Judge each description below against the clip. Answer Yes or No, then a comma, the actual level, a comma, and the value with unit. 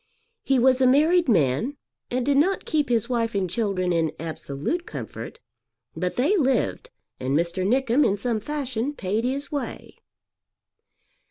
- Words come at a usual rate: Yes, average, 150 wpm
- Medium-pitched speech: No, high, 245 Hz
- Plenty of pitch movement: Yes, wide, 7.2 semitones